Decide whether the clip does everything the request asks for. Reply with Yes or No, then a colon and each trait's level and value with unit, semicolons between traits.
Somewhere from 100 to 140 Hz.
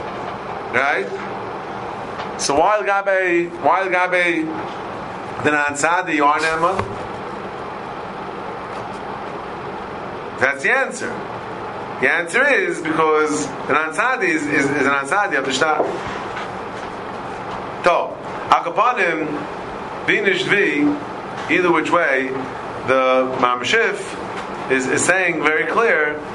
No: medium, 155 Hz